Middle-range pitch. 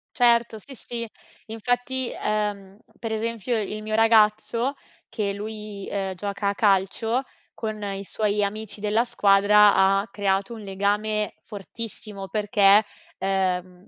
No: high, 210 Hz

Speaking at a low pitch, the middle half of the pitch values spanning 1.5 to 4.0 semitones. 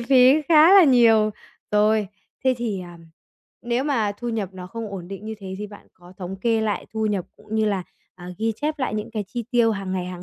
No: high, 215 Hz; average, 3.5 semitones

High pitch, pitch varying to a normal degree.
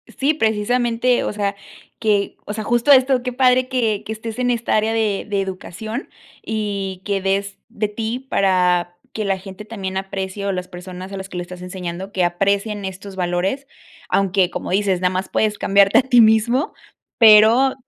Yes: high, 205 Hz; average, 3.0 semitones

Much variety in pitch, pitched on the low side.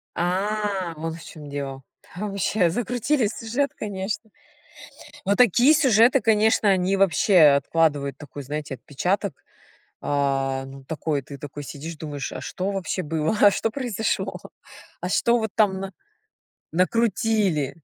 No: wide, 6.5 semitones; medium, 185 Hz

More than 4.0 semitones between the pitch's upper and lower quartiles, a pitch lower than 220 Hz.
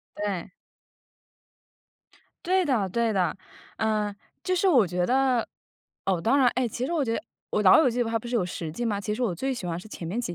No: average, 5.1 semitones; high, 225 Hz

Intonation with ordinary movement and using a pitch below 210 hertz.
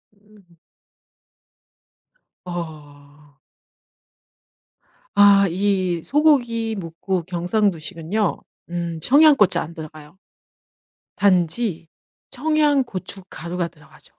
Yes: average, 4.3 semitones; medium, 185 Hz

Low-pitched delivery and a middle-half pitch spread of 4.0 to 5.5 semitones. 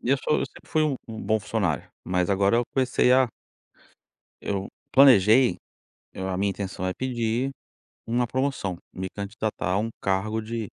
Yes: low, 110 Hz; average, 4.3 semitones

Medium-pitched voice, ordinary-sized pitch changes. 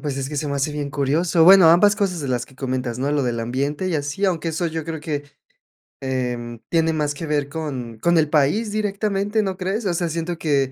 Yes: medium, 150 Hz; average, 4.2 semitones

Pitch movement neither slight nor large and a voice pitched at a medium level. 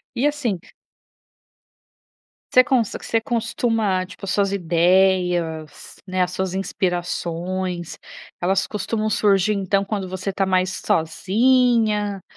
No: average, 3.0 semitones; high, 195 Hz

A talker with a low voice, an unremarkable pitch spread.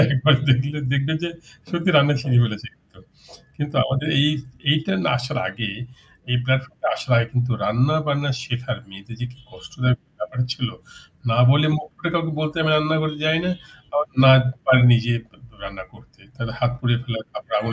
Yes: low, 130 Hz; average, 3.9 semitones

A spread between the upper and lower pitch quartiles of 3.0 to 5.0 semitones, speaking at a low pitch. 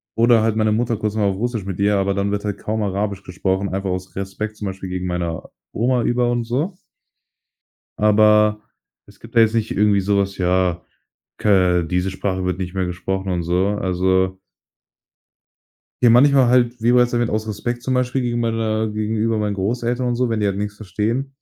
Yes: average, 3.5 semitones; low, 105 Hz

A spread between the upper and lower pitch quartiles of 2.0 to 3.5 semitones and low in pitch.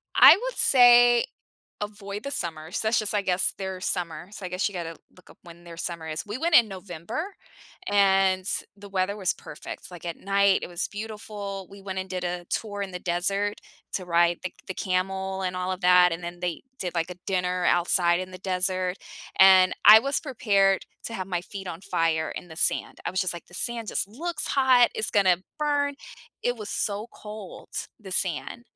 No: average, 2.7 semitones; high, 190 Hz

